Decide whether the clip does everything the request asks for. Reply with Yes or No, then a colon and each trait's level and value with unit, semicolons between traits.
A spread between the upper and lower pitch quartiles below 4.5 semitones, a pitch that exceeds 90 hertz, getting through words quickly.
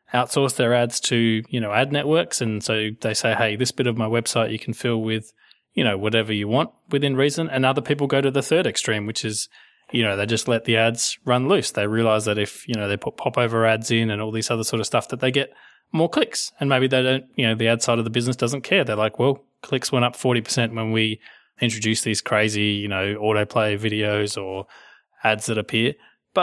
Yes: average, 2.8 semitones; low, 115 Hz; fast, 240 wpm